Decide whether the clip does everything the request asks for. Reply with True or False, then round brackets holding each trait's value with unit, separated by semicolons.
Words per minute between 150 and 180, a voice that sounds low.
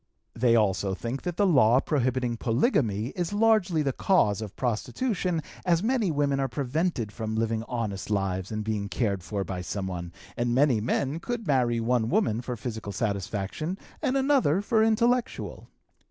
True (160 wpm; 125 Hz)